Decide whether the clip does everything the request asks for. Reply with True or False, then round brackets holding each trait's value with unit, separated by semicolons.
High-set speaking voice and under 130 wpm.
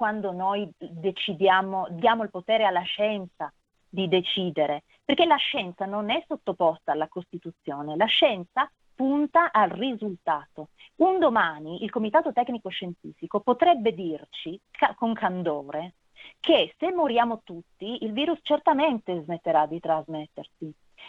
True (195 Hz; 120 wpm)